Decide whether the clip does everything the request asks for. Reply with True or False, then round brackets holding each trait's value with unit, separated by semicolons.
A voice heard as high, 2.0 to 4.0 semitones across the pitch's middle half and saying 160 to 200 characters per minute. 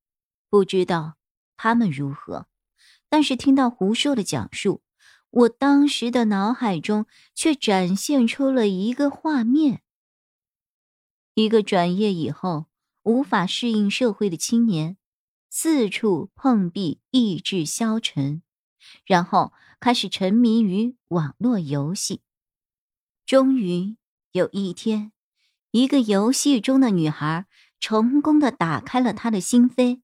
False (220 Hz; 5.3 semitones; 180 characters per minute)